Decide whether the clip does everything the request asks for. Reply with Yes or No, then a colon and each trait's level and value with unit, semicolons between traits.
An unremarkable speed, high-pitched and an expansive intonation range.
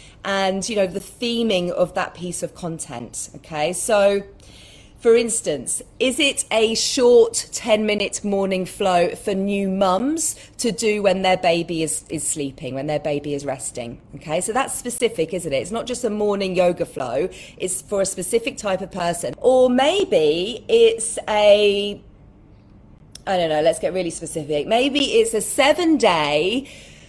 Yes: average, 165 wpm; high, 195 Hz; wide, 5.8 semitones